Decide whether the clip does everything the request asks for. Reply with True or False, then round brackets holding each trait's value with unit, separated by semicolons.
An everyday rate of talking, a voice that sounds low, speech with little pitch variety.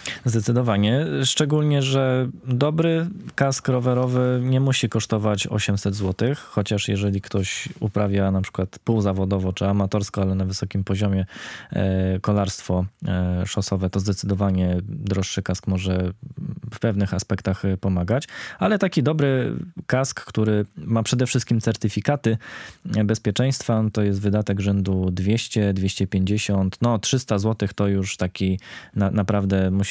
False (120 wpm; 105 Hz; 4.5 semitones)